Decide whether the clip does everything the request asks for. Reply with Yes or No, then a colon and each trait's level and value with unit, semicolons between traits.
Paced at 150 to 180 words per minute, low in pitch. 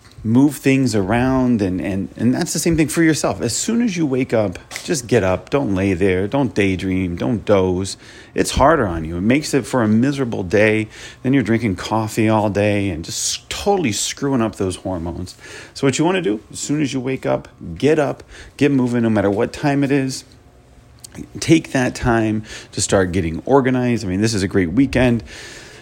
No: fast, 205 wpm; low, 115 Hz